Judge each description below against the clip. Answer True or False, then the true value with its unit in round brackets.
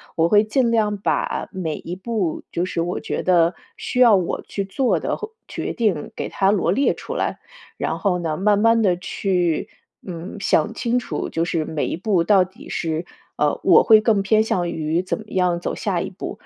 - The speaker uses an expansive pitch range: False (3.9 semitones)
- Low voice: False (190 Hz)